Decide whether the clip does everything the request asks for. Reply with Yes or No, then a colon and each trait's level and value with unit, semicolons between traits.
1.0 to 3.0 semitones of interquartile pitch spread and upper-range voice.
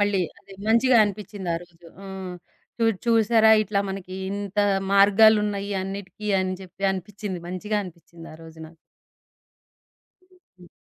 Yes: narrow, 2.5 semitones; high, 200 Hz